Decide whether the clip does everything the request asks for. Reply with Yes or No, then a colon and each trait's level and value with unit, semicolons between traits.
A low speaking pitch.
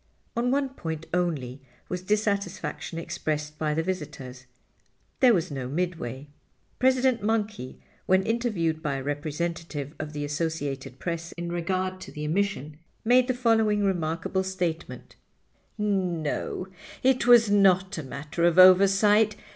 No: medium, 175 Hz